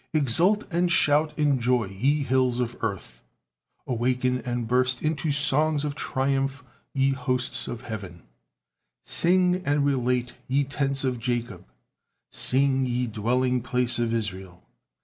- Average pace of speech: No, slow, 130 wpm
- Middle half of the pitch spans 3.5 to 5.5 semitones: No, average, 2.8 semitones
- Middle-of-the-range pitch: No, low, 130 Hz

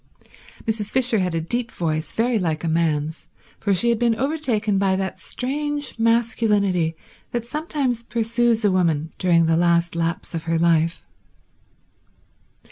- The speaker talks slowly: No, average, 145 wpm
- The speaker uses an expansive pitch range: Yes, wide, 5.9 semitones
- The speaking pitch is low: No, high, 200 Hz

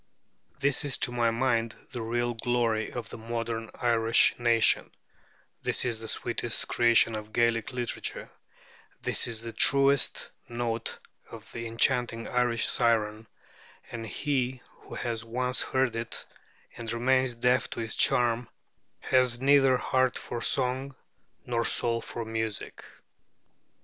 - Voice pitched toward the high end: No, low, 120 Hz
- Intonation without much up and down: Yes, narrow, 1.6 semitones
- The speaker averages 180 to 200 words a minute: No, slow, 135 wpm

